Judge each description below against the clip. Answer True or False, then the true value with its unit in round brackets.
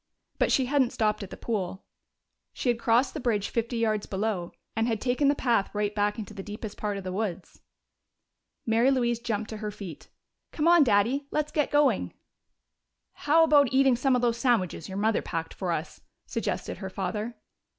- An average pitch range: True (3.9 semitones)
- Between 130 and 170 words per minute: False (190 wpm)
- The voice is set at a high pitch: True (225 Hz)